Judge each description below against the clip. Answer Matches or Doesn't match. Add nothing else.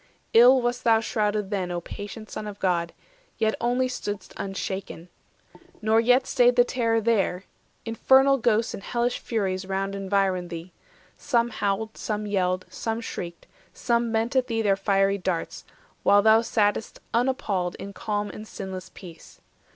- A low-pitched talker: Doesn't match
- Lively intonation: Doesn't match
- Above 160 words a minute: Doesn't match